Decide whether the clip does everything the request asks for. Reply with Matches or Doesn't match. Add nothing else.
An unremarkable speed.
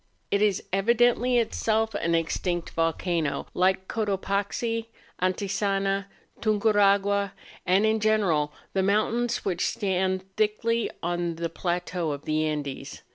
Doesn't match